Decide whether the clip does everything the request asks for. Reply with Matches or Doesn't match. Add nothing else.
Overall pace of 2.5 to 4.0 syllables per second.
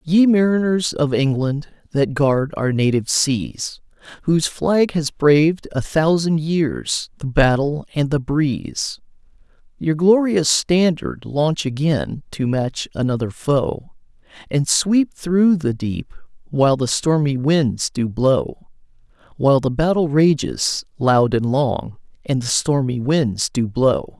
Matches